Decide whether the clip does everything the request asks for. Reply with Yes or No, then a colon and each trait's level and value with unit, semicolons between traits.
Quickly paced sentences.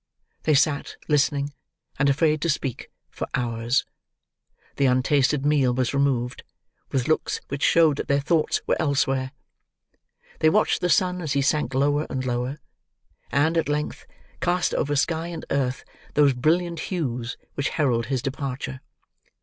No: average, 150 wpm